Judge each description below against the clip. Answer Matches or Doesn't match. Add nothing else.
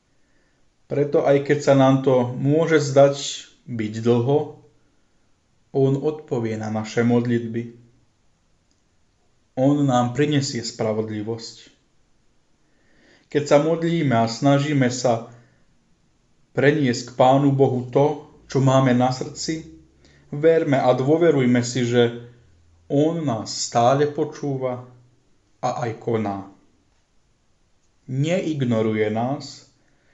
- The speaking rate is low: Matches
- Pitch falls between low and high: Doesn't match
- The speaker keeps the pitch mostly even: Doesn't match